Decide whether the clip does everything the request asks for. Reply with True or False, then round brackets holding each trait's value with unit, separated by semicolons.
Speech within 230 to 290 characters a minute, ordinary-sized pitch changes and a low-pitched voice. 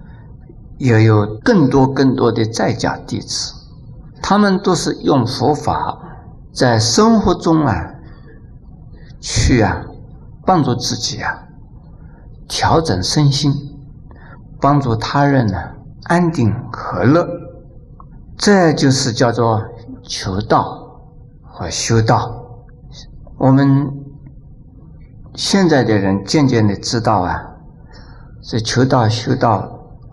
False (140 characters per minute; 4.1 semitones; 130 Hz)